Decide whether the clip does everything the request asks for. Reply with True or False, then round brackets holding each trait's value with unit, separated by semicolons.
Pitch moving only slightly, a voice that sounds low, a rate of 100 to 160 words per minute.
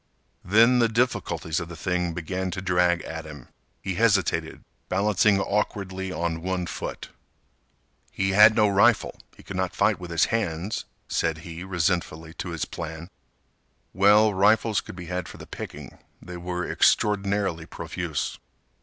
False (3.0 semitones; 90 Hz; 150 wpm)